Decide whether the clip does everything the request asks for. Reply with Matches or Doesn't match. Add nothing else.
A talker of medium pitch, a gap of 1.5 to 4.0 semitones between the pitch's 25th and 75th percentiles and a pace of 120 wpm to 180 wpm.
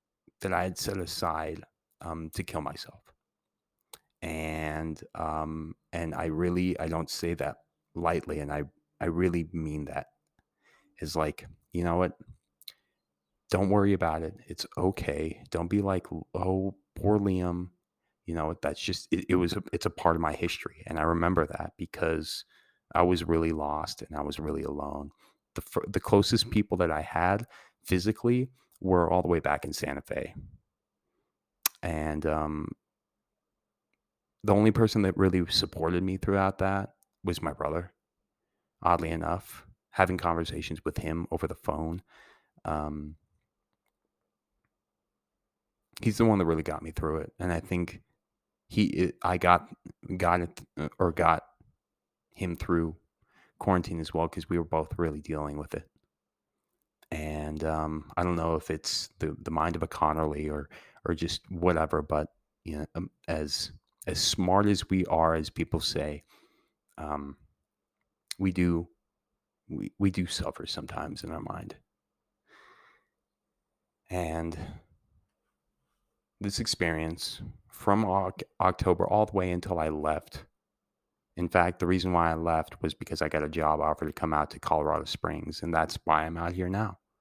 Doesn't match